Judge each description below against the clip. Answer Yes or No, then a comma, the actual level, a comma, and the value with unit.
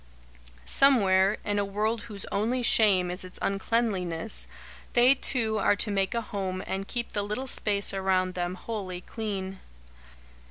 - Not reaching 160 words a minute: Yes, average, 150 wpm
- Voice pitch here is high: Yes, high, 200 Hz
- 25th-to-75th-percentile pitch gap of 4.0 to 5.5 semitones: No, average, 3.0 semitones